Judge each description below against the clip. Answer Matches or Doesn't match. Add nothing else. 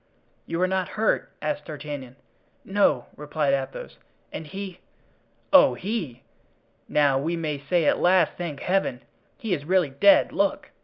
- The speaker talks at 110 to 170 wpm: Matches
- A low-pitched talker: Doesn't match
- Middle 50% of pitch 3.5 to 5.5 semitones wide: Matches